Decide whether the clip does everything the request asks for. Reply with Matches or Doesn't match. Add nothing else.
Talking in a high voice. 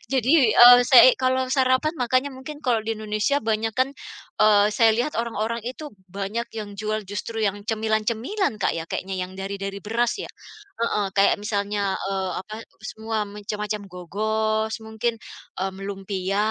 Matches